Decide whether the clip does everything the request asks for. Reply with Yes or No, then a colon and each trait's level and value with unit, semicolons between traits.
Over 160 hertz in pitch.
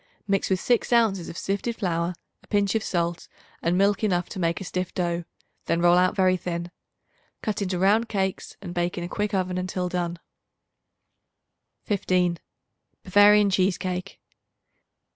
Yes: medium, 185 Hz